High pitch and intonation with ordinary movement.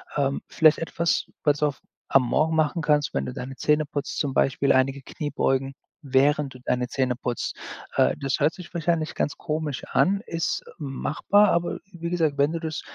No: medium, 150 Hz; average, 3.0 semitones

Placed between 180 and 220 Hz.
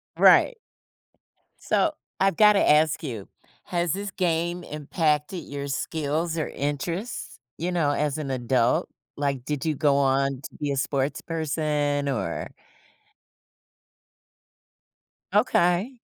No: medium, 150 Hz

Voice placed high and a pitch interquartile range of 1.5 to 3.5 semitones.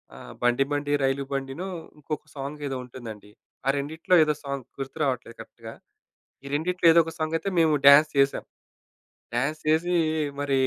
No: medium, 140 Hz; narrow, 2.6 semitones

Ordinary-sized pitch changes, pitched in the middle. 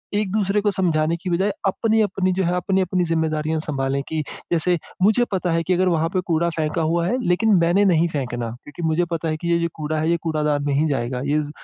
Yes: average, 3.1 semitones; medium, 170 Hz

